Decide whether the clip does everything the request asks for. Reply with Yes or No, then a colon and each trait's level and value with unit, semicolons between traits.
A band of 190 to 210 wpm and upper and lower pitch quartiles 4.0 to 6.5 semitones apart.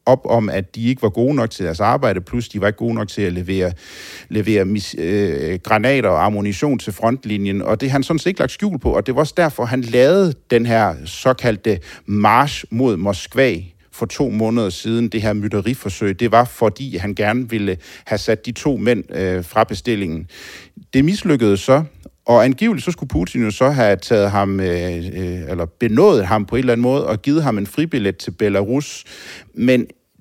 Yes: average, 205 wpm; average, 4.3 semitones